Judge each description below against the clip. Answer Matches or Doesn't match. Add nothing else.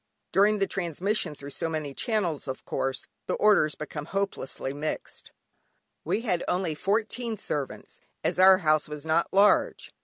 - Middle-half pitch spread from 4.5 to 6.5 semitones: Matches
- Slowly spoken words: Doesn't match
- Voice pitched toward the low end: Doesn't match